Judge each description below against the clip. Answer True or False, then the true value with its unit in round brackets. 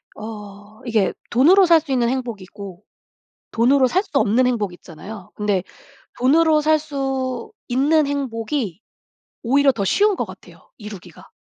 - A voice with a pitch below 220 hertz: False (250 Hz)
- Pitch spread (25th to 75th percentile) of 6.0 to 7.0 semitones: False (5.2 semitones)